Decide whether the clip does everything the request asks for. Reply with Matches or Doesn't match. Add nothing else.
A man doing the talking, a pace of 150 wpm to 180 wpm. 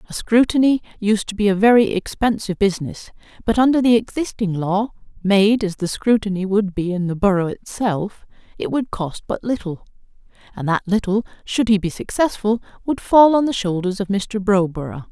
Doesn't match